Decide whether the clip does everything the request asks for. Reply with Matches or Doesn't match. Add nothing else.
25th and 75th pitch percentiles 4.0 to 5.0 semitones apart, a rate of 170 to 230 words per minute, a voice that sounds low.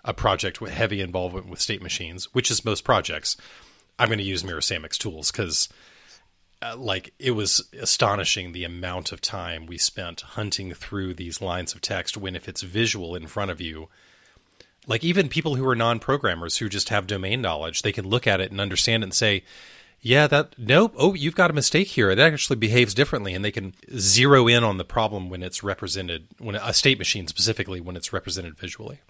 Matches